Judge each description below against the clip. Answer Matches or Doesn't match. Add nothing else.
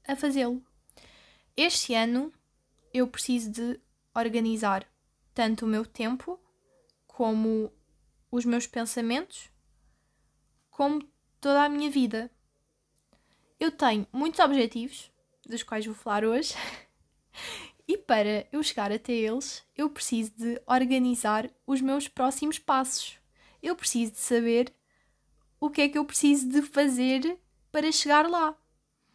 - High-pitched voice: Matches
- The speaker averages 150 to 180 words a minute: Doesn't match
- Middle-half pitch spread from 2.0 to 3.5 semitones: Doesn't match